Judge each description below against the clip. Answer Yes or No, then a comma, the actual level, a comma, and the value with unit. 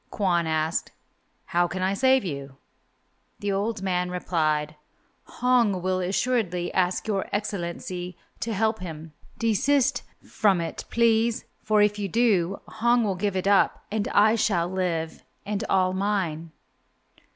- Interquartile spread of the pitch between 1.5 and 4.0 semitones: Yes, average, 3.7 semitones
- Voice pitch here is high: Yes, high, 195 Hz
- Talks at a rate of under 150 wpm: Yes, average, 140 wpm